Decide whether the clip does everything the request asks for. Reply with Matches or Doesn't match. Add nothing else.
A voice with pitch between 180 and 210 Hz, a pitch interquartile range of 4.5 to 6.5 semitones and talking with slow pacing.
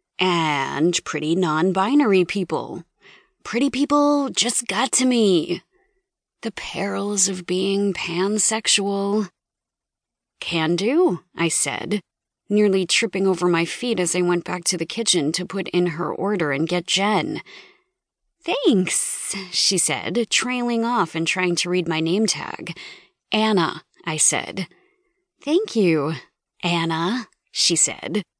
Matches